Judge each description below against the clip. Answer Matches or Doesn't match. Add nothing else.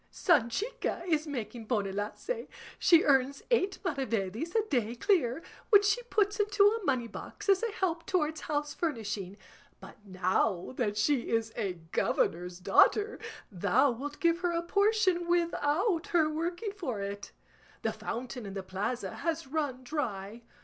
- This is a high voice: Matches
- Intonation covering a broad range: Matches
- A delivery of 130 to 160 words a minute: Matches